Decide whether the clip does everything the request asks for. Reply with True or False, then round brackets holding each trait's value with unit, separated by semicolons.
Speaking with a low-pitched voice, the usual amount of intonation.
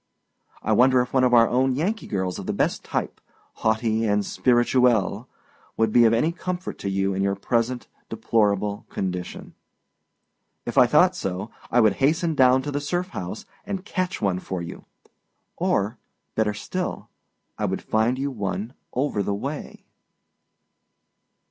True (120 Hz; 4.9 semitones)